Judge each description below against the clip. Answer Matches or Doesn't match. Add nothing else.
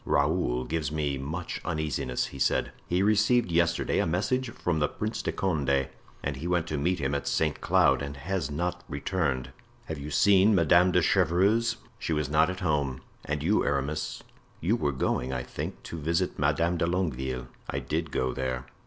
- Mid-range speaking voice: Doesn't match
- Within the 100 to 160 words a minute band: Doesn't match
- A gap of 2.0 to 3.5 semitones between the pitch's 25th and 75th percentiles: Doesn't match